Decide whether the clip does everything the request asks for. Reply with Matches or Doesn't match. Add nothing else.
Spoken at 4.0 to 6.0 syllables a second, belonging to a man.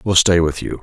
Doesn't match